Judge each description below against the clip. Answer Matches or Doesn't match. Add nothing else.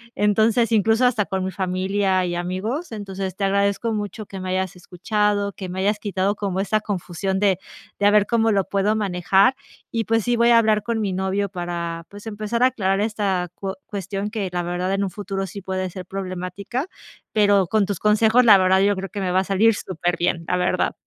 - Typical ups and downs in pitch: Doesn't match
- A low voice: Doesn't match